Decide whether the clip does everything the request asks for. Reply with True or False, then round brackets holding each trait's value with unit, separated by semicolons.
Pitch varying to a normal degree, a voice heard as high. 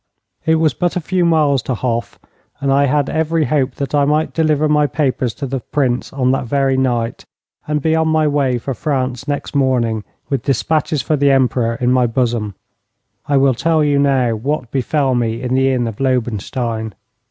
False (3.2 semitones; 135 Hz)